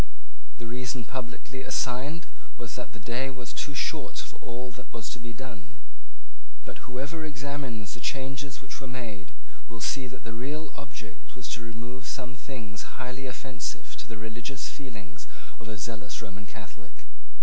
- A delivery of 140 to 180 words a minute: Yes, average, 165 wpm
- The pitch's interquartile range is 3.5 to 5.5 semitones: No, average, 2.8 semitones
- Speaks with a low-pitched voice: Yes, low, 125 Hz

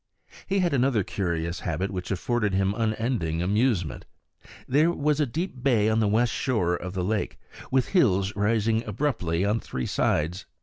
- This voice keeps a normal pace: Yes, average, 165 wpm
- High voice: No, low, 105 Hz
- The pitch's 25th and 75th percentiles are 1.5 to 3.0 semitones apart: No, wide, 5.5 semitones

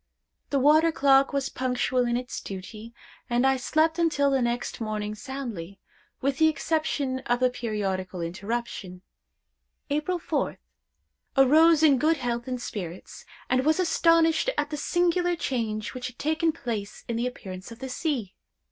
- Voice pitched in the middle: No, very high, 255 Hz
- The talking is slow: No, average, 150 wpm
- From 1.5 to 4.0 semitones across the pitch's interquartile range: No, average, 5.2 semitones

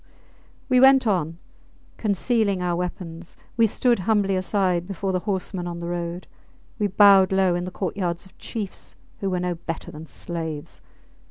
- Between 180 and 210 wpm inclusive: No, average, 160 wpm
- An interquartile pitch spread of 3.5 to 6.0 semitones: No, average, 2.7 semitones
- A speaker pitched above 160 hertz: Yes, medium, 185 Hz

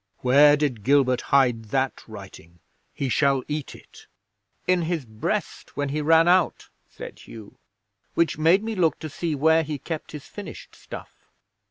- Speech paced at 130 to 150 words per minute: No, average, 160 wpm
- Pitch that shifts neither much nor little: Yes, average, 4.0 semitones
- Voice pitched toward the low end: No, medium, 145 Hz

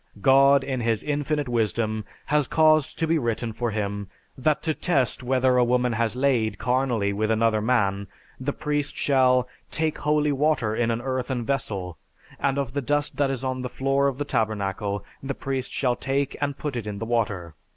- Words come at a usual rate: Yes, average, 190 wpm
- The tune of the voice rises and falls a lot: No, average, 3.8 semitones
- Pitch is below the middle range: Yes, low, 130 Hz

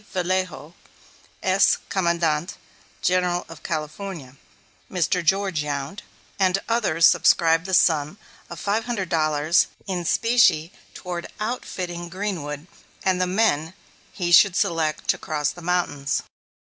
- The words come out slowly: Yes, slow, 120 wpm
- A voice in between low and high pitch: Yes, medium, 175 Hz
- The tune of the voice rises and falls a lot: No, average, 3.3 semitones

